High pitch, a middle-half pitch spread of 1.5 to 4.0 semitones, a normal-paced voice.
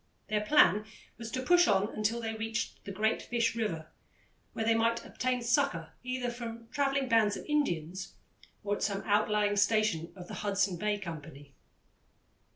Yes: high, 215 Hz; average, 2.9 semitones; average, 165 wpm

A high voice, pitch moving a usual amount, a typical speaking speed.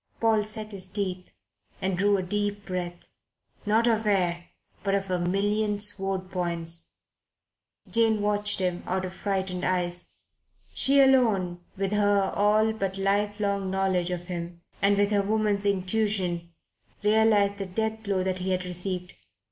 No: high, 195 Hz; narrow, 2.2 semitones; average, 150 wpm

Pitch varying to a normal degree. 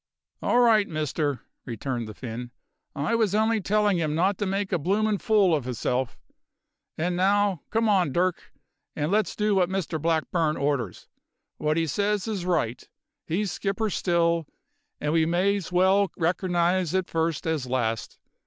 Yes: average, 4.8 semitones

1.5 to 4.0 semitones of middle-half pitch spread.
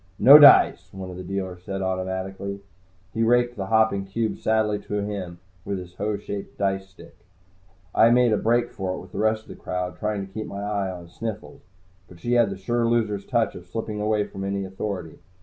Yes: narrow, 2.5 semitones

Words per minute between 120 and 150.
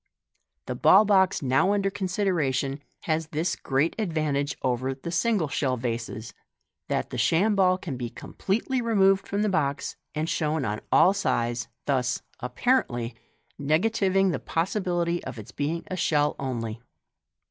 Yes: average, 145 wpm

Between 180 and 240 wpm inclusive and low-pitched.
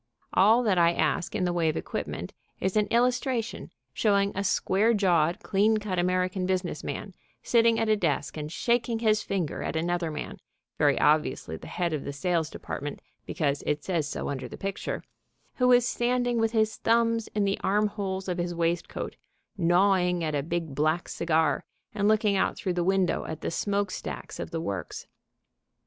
No: average, 185 wpm; medium, 185 Hz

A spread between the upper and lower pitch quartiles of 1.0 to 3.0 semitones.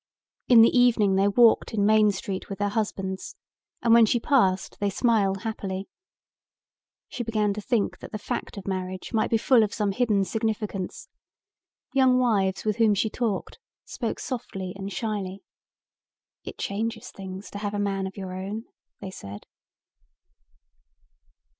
Yes: average, 2.7 semitones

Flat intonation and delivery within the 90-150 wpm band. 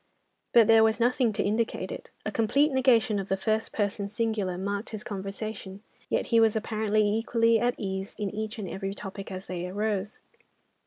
No: narrow, 2.3 semitones; average, 180 wpm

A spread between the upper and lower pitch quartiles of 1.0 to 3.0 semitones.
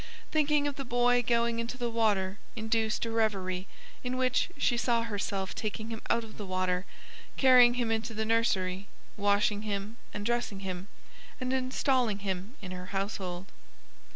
No: average, 3.5 semitones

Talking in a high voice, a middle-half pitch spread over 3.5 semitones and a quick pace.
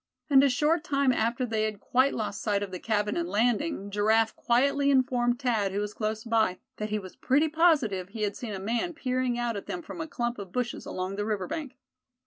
Yes: high, 230 Hz; average, 4.1 semitones; fast, 225 wpm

